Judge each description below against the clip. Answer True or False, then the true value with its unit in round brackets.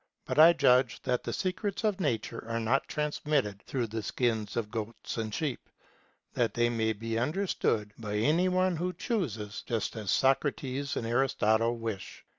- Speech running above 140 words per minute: True (165 wpm)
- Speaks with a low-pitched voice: True (120 Hz)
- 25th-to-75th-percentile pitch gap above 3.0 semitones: True (5.2 semitones)